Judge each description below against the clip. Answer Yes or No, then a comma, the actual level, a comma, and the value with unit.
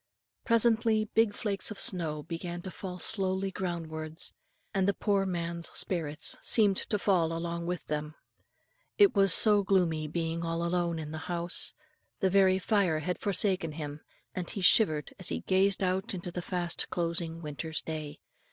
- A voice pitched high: No, medium, 175 Hz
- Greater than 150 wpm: Yes, average, 170 wpm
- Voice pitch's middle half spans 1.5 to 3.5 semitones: Yes, average, 3.0 semitones